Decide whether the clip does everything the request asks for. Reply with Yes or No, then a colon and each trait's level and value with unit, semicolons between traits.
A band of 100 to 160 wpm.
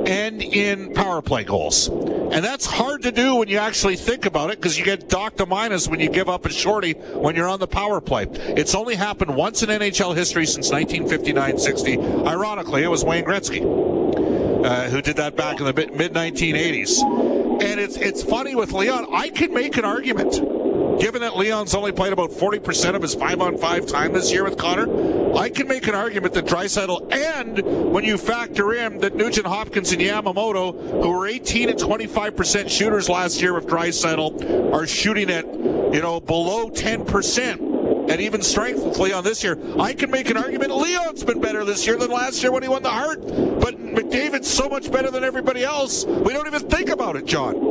No: average, 200 wpm